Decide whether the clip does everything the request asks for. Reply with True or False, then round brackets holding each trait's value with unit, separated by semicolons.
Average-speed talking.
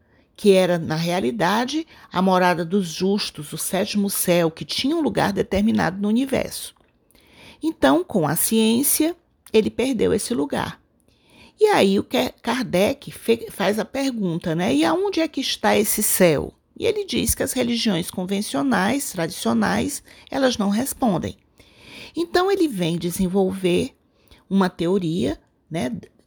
True (135 wpm)